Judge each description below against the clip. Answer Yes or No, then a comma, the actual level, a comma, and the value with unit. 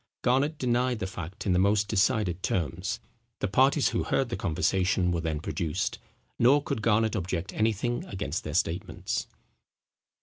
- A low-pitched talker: Yes, low, 100 Hz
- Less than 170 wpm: Yes, average, 155 wpm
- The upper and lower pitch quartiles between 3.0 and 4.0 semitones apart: No, average, 5.1 semitones